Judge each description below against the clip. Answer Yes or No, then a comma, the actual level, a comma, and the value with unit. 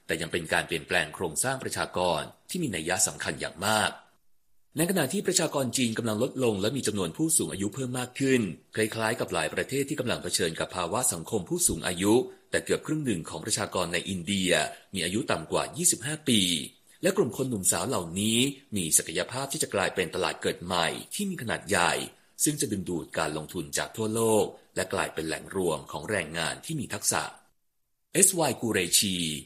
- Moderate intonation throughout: No, wide, 6.3 semitones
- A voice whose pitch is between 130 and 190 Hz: No, low, 115 Hz